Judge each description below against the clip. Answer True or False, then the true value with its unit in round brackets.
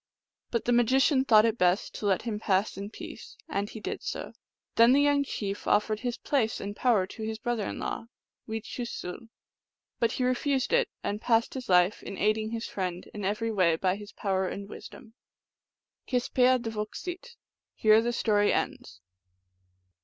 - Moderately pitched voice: False (220 Hz)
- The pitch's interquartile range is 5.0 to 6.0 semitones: False (3.3 semitones)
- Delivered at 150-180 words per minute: True (170 wpm)